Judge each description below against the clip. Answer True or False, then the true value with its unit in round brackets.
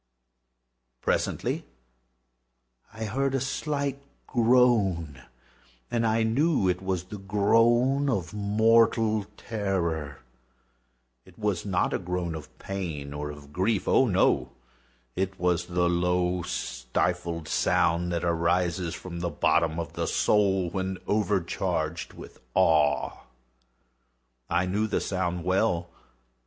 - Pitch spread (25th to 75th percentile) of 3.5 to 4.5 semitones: True (4.1 semitones)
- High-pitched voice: False (90 Hz)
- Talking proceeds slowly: True (110 wpm)